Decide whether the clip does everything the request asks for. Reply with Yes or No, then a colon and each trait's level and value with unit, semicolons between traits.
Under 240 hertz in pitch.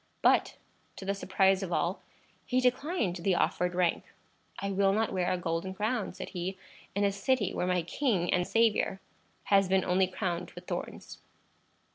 Yes: high, 190 Hz